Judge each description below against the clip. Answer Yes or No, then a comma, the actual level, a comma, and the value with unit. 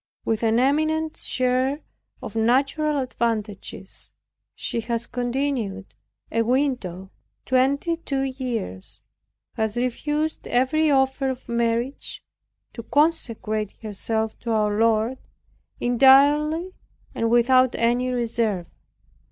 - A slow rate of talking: Yes, slow, 100 wpm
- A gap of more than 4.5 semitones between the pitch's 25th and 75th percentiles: No, average, 3.3 semitones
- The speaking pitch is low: No, very high, 250 Hz